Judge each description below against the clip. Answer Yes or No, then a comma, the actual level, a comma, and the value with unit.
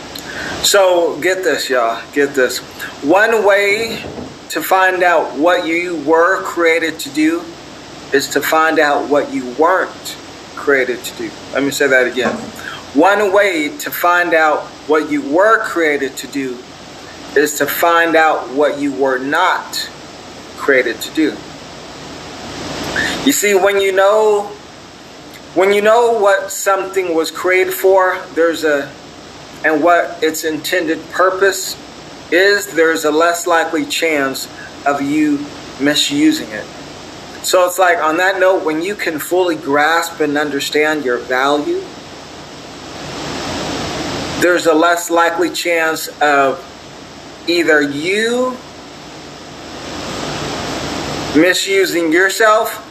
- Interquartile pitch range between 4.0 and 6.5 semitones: Yes, average, 4.5 semitones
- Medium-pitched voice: Yes, medium, 170 Hz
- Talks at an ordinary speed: No, slow, 125 wpm